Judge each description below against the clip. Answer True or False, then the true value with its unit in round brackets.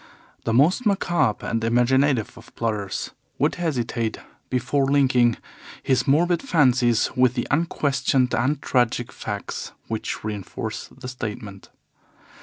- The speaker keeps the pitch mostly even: False (3.6 semitones)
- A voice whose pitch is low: True (125 Hz)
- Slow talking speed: True (115 wpm)